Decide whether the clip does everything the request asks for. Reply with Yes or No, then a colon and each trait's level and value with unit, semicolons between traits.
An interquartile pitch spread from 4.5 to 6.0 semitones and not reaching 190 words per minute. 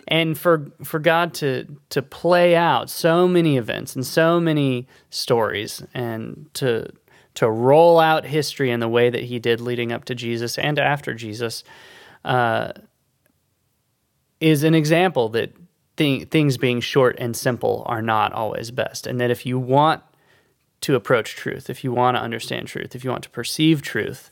Yes: average, 4.8 semitones; average, 170 wpm